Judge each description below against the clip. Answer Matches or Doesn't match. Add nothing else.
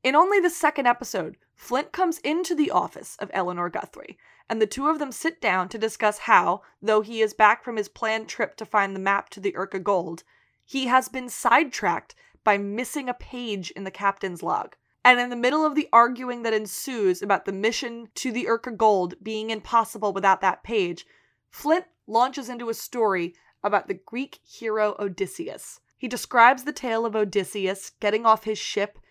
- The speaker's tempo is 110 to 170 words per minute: Doesn't match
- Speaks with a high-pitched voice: Matches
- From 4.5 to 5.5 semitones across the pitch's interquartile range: Doesn't match